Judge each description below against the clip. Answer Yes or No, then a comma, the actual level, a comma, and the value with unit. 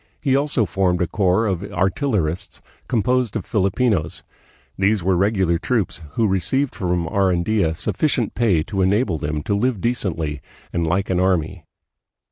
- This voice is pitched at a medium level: No, very low, 95 Hz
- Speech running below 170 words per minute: Yes, average, 145 wpm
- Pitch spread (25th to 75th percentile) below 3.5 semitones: No, average, 4.1 semitones